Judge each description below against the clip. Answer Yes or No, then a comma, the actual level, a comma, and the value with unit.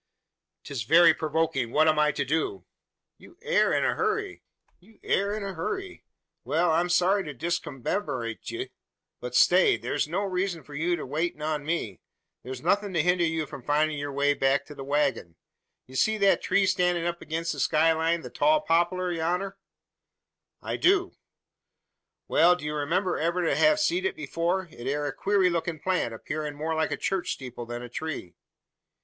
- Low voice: No, medium, 165 Hz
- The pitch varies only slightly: No, average, 4.0 semitones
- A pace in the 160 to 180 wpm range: Yes, average, 170 wpm